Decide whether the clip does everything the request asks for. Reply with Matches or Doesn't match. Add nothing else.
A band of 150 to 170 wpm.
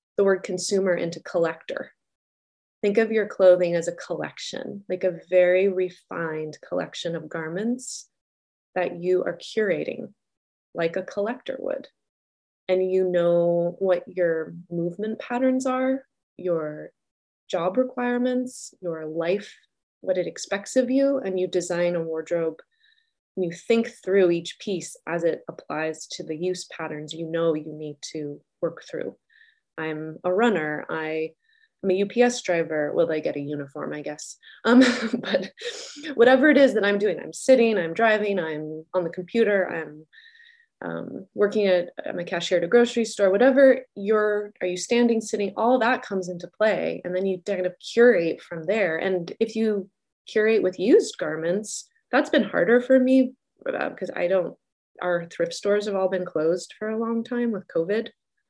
Matches